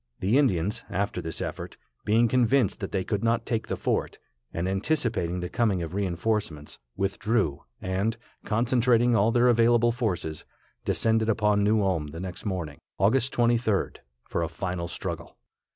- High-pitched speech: No, low, 105 Hz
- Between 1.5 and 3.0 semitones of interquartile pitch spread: No, average, 4.3 semitones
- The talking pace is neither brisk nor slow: Yes, average, 150 wpm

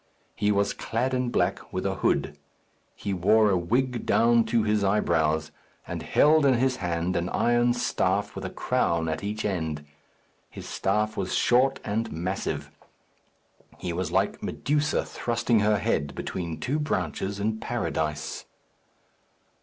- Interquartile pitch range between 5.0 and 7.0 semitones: Yes, wide, 5.5 semitones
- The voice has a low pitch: Yes, low, 105 Hz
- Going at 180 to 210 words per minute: No, average, 145 wpm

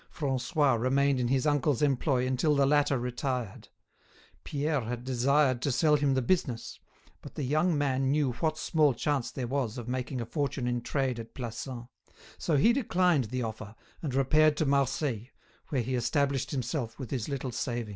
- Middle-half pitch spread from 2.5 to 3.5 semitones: Yes, average, 3.0 semitones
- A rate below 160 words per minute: No, average, 175 wpm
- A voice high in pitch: No, low, 135 Hz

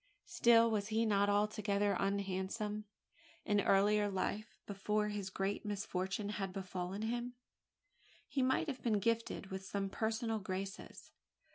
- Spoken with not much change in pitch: Yes, narrow, 2.1 semitones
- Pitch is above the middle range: Yes, high, 205 Hz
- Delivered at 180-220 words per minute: No, slow, 135 wpm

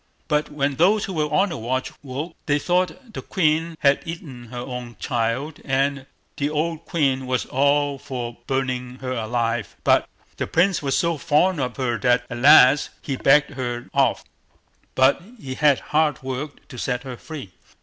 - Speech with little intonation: No, average, 3.3 semitones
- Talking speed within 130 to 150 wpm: No, average, 175 wpm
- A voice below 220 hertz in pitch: Yes, medium, 140 Hz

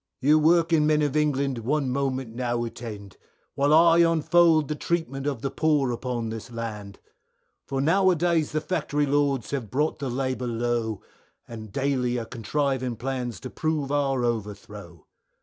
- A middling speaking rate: Yes, average, 160 wpm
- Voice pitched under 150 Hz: Yes, low, 135 Hz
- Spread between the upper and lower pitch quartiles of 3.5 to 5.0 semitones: Yes, average, 4.2 semitones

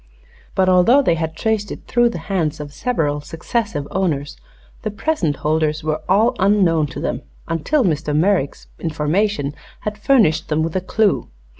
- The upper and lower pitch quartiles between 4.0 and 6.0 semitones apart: Yes, wide, 5.5 semitones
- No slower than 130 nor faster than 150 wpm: No, average, 160 wpm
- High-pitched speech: No, medium, 170 Hz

